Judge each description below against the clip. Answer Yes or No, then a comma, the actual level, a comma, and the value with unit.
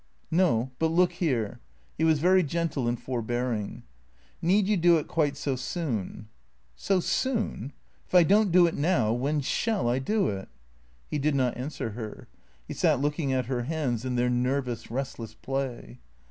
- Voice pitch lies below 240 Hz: Yes, low, 135 Hz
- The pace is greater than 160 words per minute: Yes, average, 190 wpm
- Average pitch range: No, wide, 5.8 semitones